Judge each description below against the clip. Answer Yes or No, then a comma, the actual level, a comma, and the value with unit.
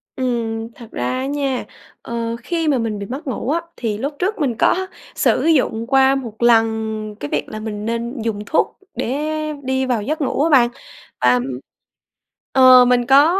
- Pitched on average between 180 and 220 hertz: No, high, 245 Hz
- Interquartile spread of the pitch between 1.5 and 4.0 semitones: Yes, average, 3.4 semitones